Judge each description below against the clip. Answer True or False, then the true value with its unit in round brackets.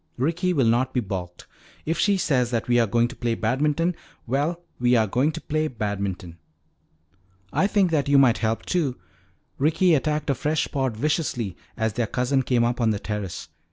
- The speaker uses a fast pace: False (190 wpm)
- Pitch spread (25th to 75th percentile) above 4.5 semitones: True (5.2 semitones)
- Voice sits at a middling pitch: False (125 Hz)